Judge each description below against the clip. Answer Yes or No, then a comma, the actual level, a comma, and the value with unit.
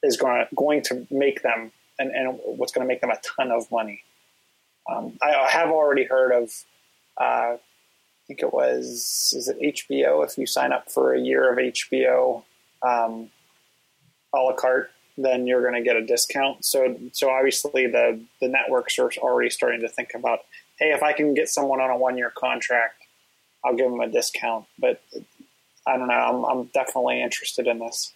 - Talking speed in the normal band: Yes, average, 190 wpm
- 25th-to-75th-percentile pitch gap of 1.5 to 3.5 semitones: No, average, 4.4 semitones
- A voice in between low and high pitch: No, low, 130 Hz